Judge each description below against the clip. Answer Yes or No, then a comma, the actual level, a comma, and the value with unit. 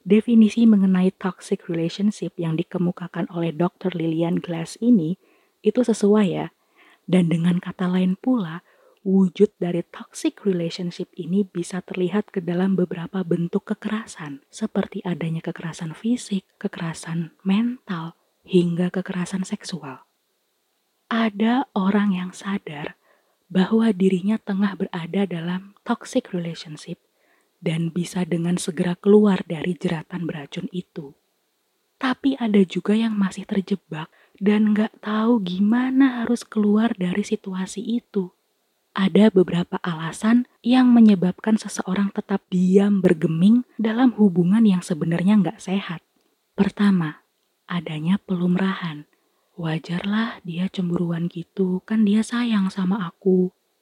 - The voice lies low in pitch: No, high, 190 Hz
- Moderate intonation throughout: Yes, average, 3.1 semitones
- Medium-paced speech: Yes, average, 115 wpm